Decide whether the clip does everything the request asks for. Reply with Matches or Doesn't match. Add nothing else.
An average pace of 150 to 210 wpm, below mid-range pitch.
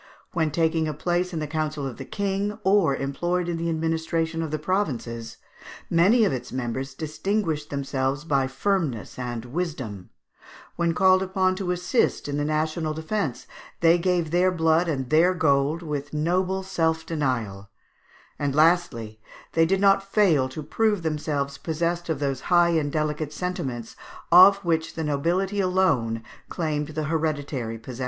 Doesn't match